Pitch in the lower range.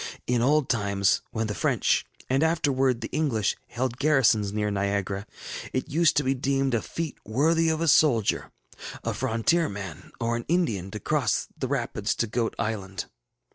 Yes: low, 120 Hz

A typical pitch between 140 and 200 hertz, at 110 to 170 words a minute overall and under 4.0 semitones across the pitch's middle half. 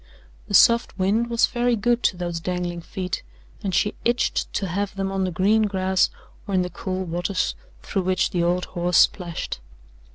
No: high, 190 Hz; average, 185 wpm; narrow, 2.4 semitones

